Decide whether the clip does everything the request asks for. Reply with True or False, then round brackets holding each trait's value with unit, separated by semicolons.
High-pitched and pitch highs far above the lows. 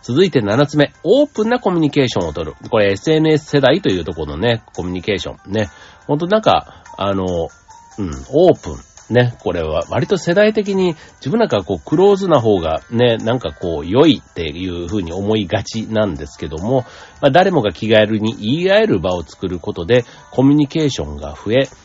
False (115 Hz; 7.7 semitones)